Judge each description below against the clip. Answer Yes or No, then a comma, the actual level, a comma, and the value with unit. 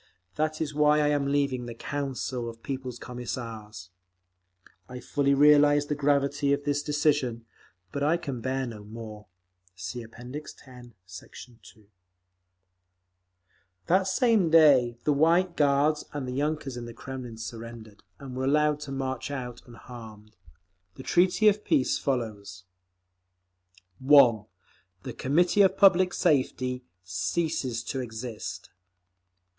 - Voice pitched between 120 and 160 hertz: Yes, low, 135 Hz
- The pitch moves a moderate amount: Yes, average, 4.0 semitones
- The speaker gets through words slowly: Yes, slow, 130 wpm